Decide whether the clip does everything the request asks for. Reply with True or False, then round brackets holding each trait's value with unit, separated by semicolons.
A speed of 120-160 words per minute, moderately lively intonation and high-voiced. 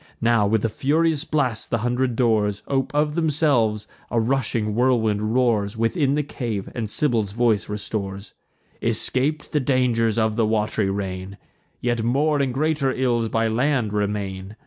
False (150 wpm; 4.0 semitones; 115 Hz)